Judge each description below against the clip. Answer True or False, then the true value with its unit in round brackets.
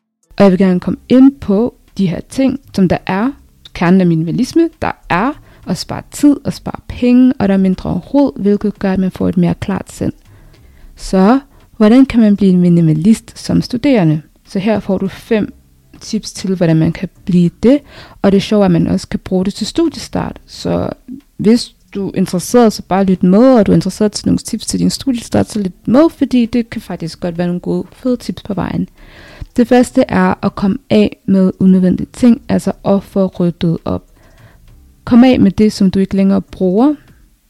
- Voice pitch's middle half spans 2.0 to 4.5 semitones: False (5.0 semitones)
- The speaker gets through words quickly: False (205 wpm)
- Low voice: False (195 Hz)